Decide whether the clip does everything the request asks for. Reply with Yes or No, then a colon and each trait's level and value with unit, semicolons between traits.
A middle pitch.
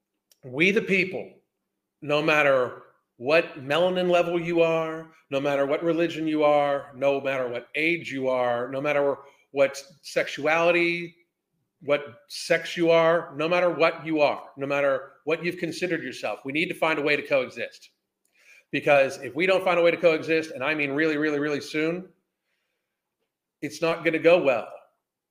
Yes: medium, 160 Hz